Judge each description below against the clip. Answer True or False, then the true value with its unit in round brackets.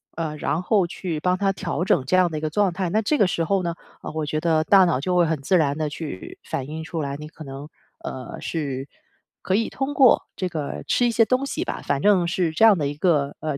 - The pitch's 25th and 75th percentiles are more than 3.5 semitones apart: True (4.0 semitones)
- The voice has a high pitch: False (165 Hz)